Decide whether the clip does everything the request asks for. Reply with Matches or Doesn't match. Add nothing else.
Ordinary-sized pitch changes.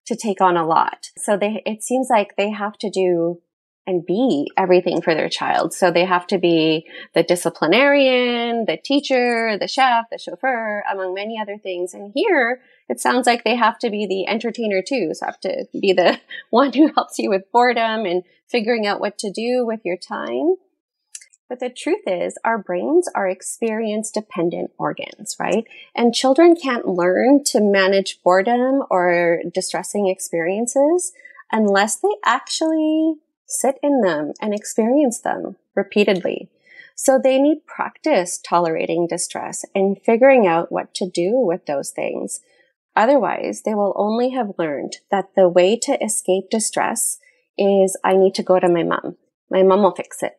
Doesn't match